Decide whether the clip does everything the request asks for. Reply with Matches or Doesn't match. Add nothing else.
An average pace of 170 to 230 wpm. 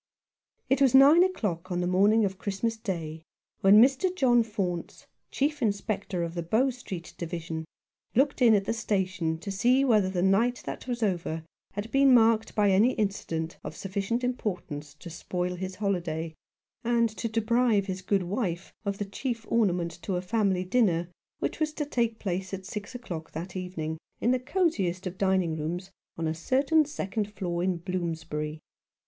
Matches